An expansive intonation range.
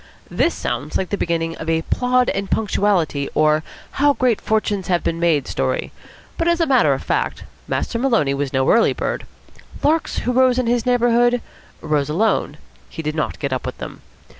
Yes: wide, 8.0 semitones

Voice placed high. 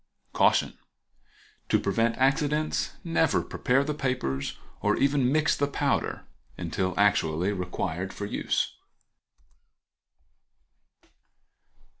No: low, 130 Hz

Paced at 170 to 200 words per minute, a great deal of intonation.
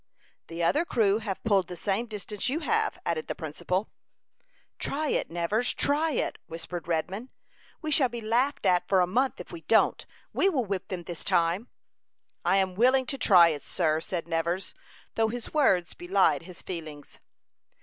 Yes: average, 175 wpm; wide, 6.0 semitones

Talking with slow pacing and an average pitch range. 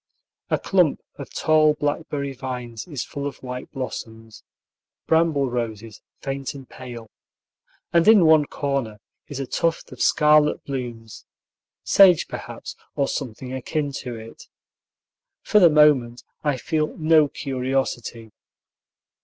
Yes: slow, 125 wpm; average, 3.8 semitones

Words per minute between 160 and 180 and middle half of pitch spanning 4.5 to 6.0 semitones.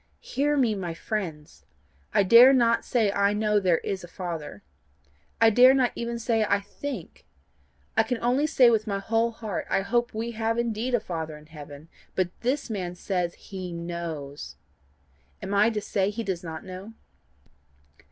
Yes: average, 170 wpm; average, 4.8 semitones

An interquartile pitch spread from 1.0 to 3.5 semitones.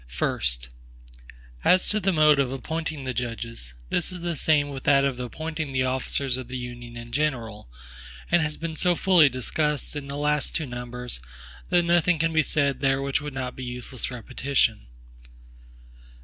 No: average, 4.1 semitones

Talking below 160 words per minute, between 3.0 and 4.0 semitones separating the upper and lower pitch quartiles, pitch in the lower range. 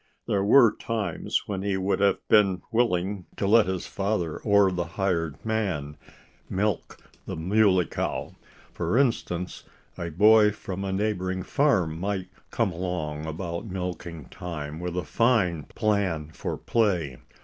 Yes: average, 140 wpm; average, 3.5 semitones; very low, 95 Hz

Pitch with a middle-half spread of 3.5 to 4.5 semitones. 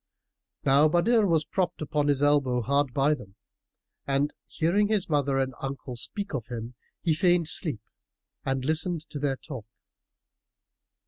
Yes: average, 3.8 semitones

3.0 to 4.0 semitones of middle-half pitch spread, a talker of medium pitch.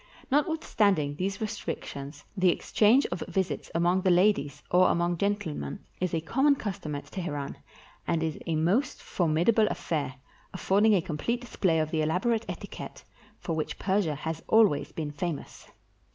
No: average, 4.9 semitones; medium, 175 Hz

